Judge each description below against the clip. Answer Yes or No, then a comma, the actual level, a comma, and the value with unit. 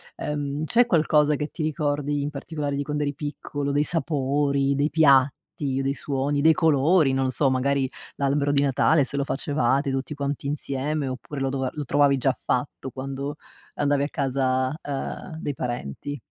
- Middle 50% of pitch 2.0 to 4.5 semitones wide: No, narrow, 1.6 semitones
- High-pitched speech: No, medium, 140 Hz